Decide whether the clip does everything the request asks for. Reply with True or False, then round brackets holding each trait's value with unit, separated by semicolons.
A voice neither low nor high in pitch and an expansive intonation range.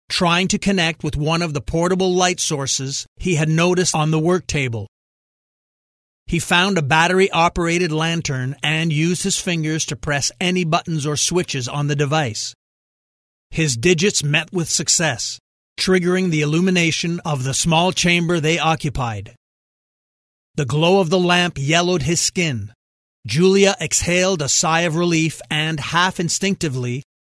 False (160 Hz; 3.5 semitones)